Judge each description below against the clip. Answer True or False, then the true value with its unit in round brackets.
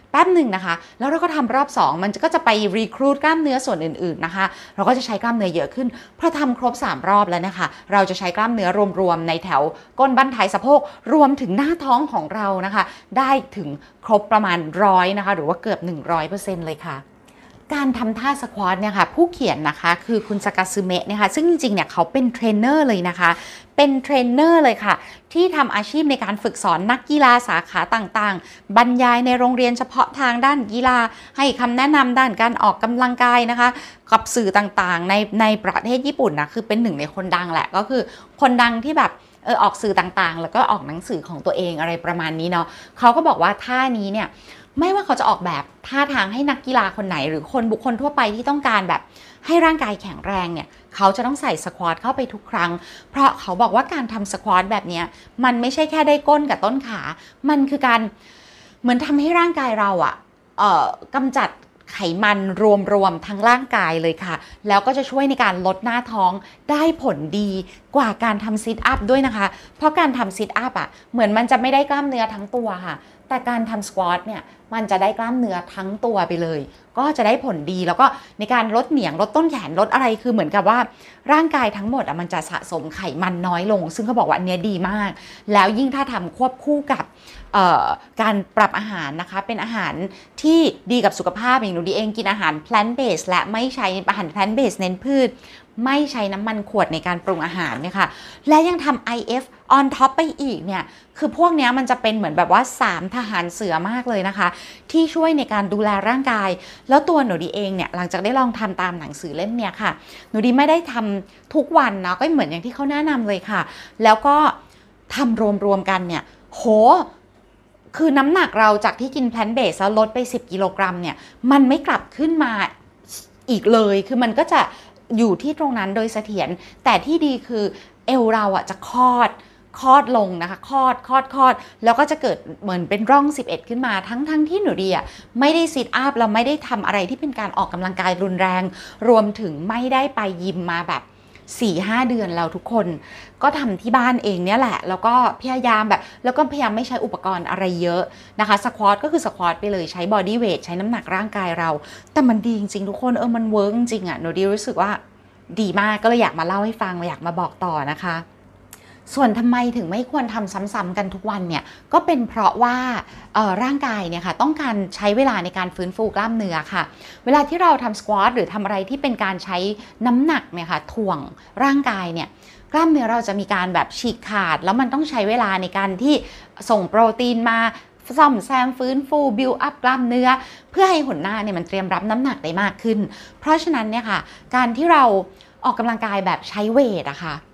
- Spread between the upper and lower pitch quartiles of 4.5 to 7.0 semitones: True (5.4 semitones)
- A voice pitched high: True (220 Hz)